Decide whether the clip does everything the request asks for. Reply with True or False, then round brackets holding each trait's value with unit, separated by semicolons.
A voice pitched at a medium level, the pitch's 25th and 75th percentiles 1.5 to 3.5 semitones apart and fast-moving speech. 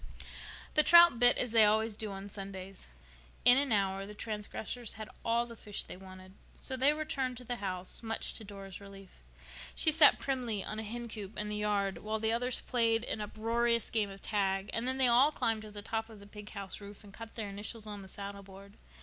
False (215 Hz; 2.9 semitones; 215 wpm)